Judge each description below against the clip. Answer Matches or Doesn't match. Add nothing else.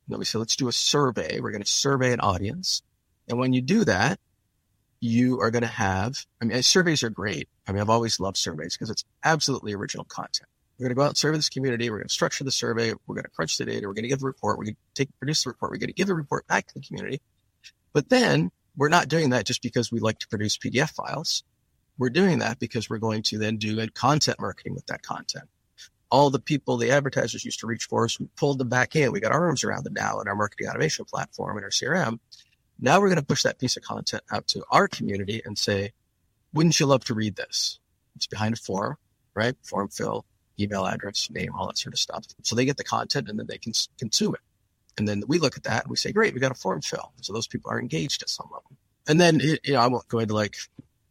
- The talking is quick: Matches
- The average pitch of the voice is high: Doesn't match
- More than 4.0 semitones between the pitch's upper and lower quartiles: Matches